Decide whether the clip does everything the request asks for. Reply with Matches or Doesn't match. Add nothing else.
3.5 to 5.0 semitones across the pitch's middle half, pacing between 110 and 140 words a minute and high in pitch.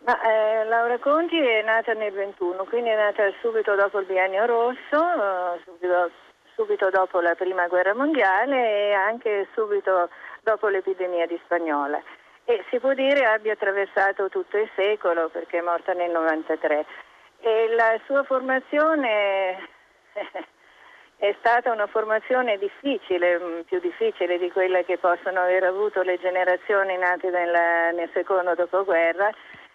Matches